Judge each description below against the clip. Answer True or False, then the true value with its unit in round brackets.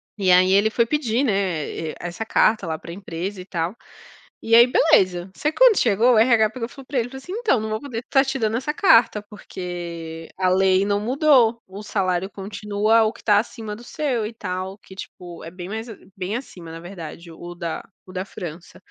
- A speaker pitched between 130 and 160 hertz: False (205 Hz)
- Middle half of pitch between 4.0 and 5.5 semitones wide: True (4.3 semitones)